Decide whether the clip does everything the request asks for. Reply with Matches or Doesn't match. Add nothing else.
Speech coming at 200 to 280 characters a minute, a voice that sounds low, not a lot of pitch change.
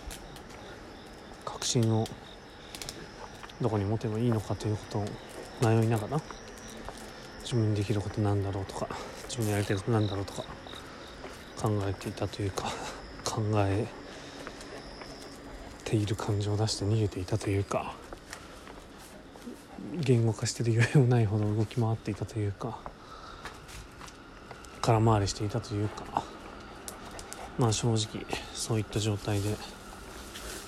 Matches